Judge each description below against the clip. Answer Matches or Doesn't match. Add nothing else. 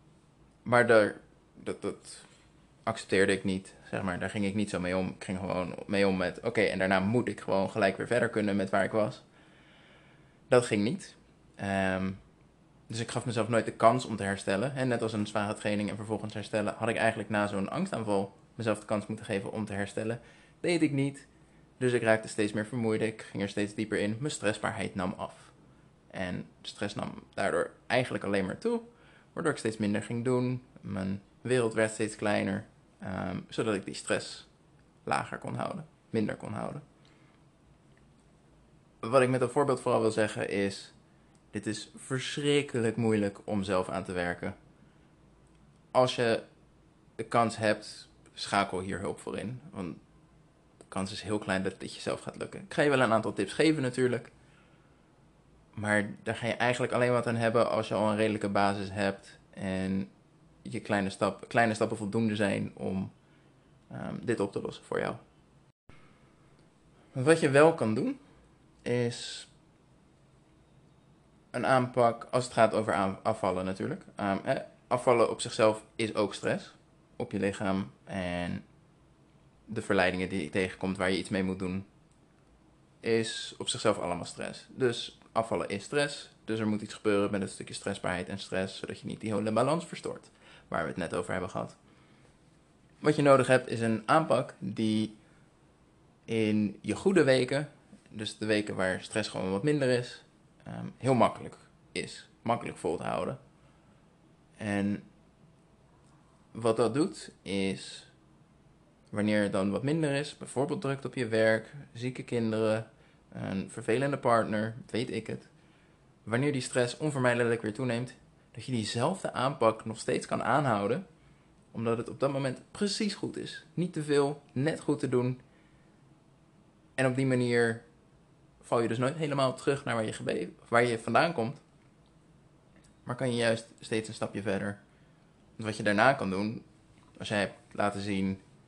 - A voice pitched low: Matches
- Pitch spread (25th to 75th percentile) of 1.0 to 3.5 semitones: Doesn't match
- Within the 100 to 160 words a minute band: Doesn't match